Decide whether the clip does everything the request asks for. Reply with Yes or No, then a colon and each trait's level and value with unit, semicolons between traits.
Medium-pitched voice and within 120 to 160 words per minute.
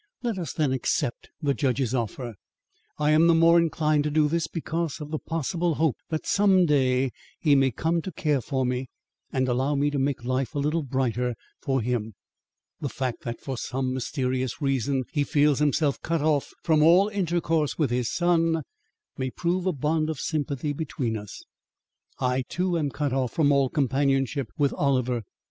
No: medium, 145 Hz; average, 180 wpm